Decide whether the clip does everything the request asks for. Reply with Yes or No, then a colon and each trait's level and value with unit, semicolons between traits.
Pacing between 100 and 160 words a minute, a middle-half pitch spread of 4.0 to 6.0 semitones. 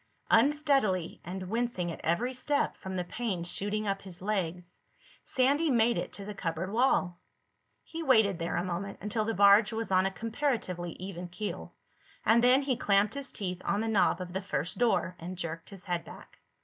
No: average, 190 wpm; average, 4.4 semitones